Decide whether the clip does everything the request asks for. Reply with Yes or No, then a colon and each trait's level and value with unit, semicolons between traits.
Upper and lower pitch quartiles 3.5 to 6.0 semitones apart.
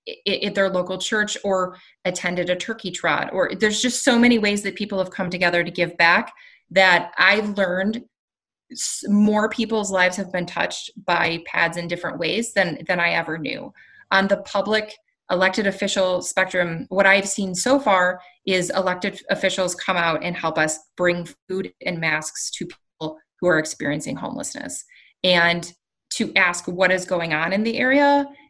No: average, 2.8 semitones